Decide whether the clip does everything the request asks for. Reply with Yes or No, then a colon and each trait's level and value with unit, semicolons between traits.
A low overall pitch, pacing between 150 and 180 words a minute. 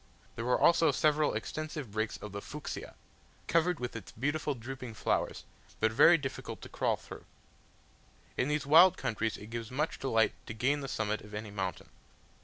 Yes: low, 125 Hz; average, 175 wpm